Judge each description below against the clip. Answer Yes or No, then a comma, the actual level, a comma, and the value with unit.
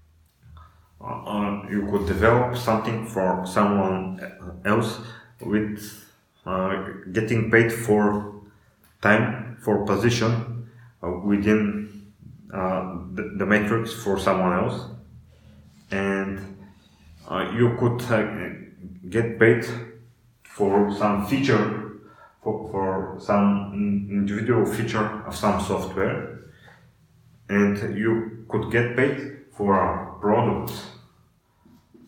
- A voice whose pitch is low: Yes, low, 105 Hz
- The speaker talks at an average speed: No, slow, 95 wpm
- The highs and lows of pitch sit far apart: No, narrow, 2.5 semitones